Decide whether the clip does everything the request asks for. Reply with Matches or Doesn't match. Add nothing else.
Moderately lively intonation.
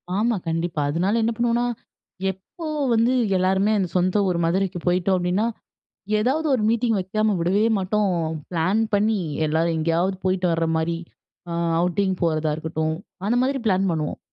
Matches